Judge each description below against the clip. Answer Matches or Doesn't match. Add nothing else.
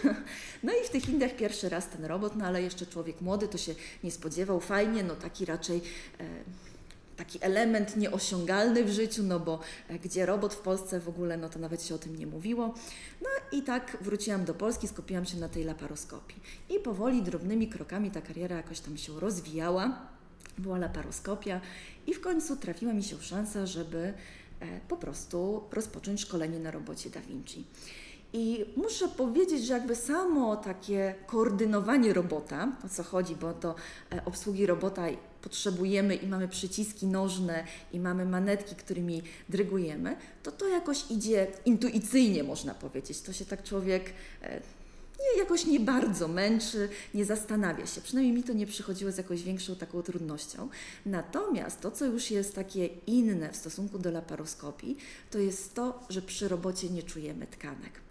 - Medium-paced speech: Doesn't match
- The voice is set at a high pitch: Matches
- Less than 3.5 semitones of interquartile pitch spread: Doesn't match